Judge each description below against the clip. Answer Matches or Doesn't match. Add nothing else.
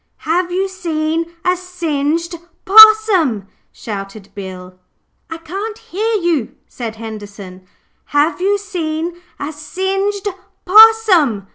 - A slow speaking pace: Matches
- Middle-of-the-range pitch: Doesn't match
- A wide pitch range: Matches